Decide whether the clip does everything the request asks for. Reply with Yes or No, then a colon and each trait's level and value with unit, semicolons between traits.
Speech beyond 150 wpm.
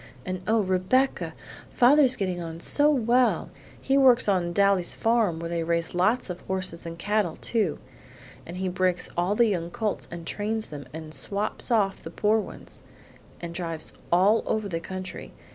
Yes: average, 170 wpm